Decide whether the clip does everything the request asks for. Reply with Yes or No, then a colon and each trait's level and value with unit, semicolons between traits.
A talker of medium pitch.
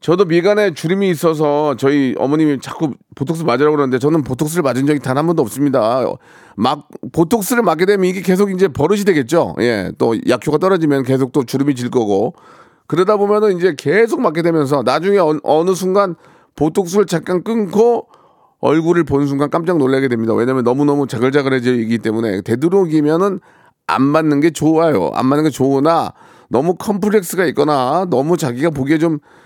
Yes: medium, 155 Hz